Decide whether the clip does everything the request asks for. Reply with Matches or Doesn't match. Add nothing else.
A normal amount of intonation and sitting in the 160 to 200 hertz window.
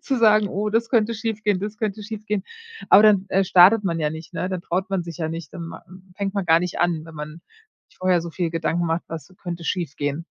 Matches